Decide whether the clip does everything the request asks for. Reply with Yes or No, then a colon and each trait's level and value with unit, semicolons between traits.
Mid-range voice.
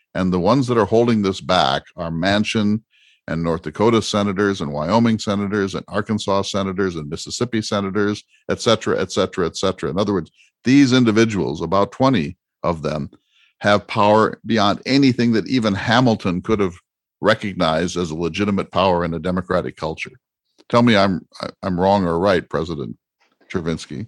No: low, 100 Hz